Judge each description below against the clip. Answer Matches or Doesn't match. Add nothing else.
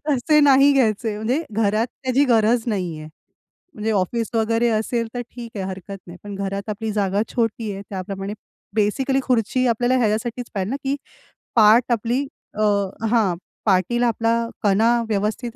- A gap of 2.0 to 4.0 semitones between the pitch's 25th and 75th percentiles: Matches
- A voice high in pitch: Matches